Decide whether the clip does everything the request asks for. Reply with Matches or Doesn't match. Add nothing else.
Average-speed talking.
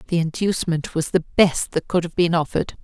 Doesn't match